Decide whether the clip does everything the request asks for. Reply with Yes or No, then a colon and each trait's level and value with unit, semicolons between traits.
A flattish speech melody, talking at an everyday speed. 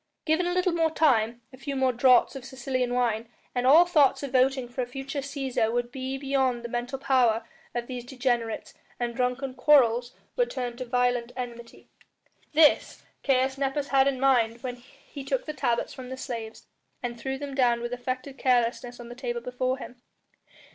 Yes: narrow, 2.0 semitones; average, 185 wpm